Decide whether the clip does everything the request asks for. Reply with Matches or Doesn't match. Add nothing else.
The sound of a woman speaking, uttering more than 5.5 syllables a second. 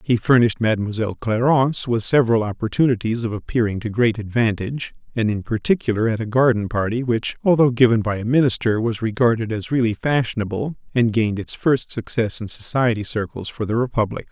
Doesn't match